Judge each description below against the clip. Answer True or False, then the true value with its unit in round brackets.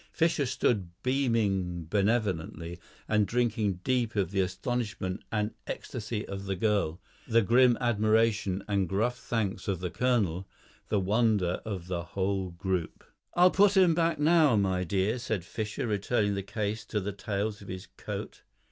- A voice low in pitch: True (105 Hz)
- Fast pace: False (155 wpm)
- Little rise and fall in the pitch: False (3.8 semitones)